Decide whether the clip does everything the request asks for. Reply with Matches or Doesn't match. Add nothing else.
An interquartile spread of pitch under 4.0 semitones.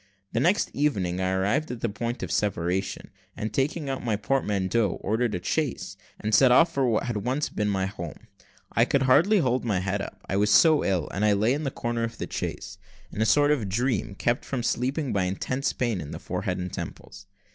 Doesn't match